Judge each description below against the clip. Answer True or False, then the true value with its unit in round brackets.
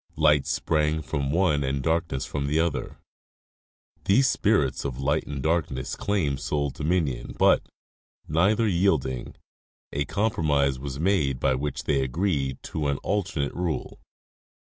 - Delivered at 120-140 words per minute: True (135 wpm)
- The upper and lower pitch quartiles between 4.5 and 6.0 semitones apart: False (3.8 semitones)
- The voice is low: True (75 Hz)